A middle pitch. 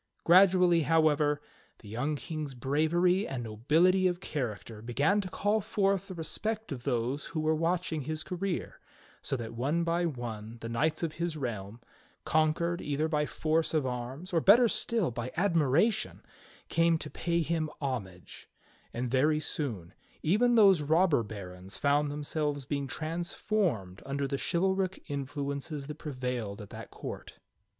Yes: medium, 150 Hz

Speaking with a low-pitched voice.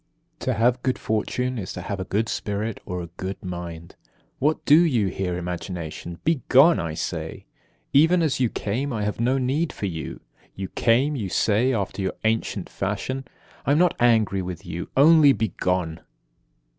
Yes: low, 110 Hz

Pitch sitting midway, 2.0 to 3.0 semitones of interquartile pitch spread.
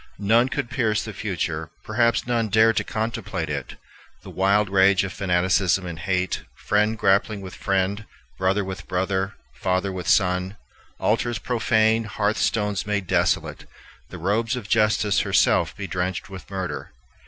No: low, 100 Hz; average, 2.7 semitones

